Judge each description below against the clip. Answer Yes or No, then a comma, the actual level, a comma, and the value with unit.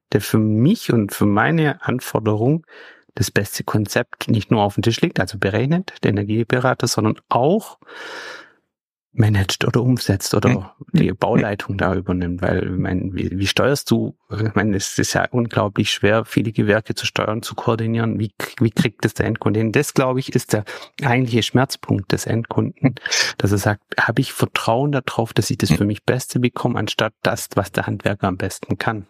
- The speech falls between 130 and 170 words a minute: No, average, 180 wpm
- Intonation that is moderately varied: Yes, average, 3.3 semitones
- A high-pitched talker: No, low, 115 Hz